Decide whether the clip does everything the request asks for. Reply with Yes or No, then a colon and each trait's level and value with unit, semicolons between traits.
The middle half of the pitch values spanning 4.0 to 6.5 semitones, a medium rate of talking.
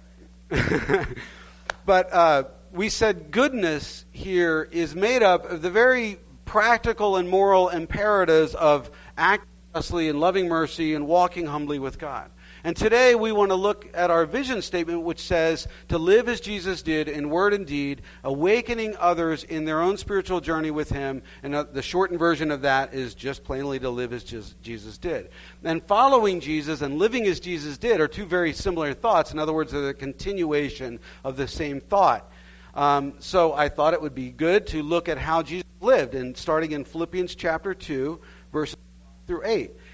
Yes: average, 4.8 semitones; average, 180 wpm